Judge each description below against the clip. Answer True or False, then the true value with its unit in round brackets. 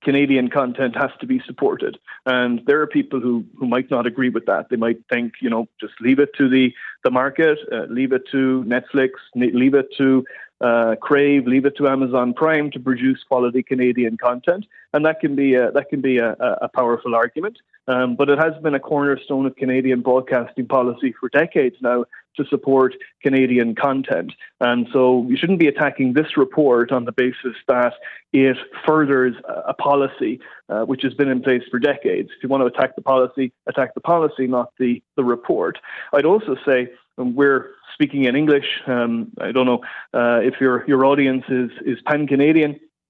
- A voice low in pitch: True (130 Hz)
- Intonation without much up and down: True (2.2 semitones)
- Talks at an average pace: True (190 wpm)